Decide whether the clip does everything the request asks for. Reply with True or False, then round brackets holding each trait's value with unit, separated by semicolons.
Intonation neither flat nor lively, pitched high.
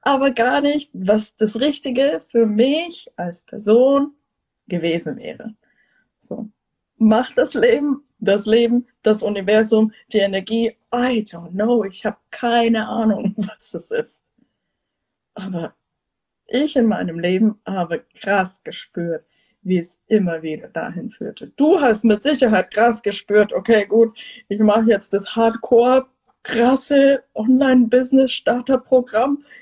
True (3.5 semitones; 225 Hz)